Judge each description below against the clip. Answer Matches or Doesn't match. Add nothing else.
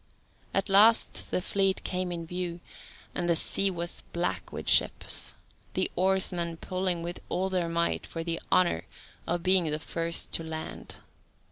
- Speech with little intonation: Matches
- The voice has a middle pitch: Matches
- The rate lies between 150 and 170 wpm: Matches